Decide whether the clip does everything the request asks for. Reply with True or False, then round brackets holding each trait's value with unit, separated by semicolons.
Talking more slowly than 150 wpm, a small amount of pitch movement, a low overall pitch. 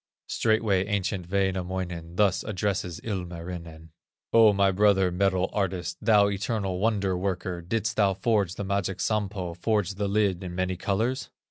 True (140 wpm; 2.3 semitones; 95 Hz)